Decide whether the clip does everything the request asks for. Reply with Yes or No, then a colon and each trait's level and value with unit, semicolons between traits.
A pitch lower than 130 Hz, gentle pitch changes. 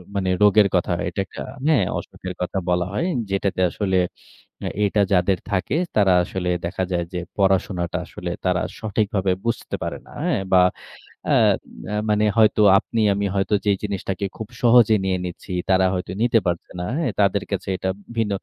Yes: very low, 95 Hz; narrow, 2.3 semitones